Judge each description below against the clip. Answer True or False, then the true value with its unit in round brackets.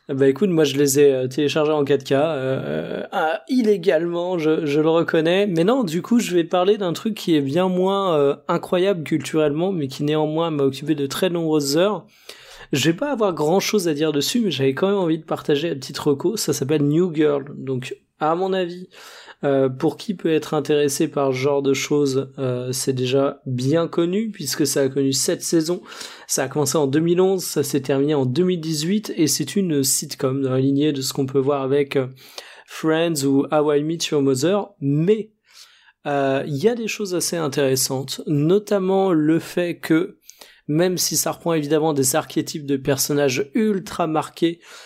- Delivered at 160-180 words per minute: False (195 wpm)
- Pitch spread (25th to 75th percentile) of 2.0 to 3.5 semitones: False (4.1 semitones)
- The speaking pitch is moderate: True (155 Hz)